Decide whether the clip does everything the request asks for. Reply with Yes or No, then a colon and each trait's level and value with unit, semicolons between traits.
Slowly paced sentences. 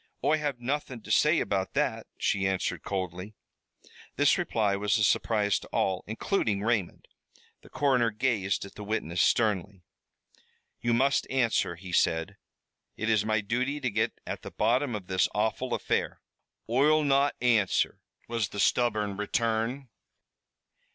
No: average, 145 wpm